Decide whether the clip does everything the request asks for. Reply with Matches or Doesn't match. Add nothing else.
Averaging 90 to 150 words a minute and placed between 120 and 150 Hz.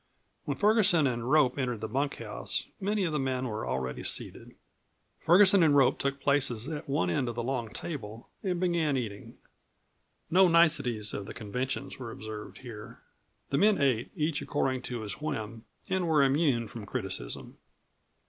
Doesn't match